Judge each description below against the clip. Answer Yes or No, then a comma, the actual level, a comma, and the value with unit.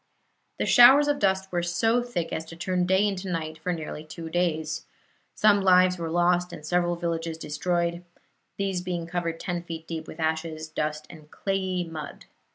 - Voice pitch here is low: No, medium, 175 Hz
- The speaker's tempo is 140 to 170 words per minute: No, average, 180 wpm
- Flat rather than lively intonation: Yes, narrow, 2.3 semitones